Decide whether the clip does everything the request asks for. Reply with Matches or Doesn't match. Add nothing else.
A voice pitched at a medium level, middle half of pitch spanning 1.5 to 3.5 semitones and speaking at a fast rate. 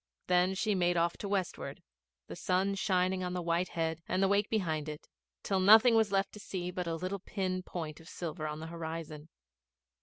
Matches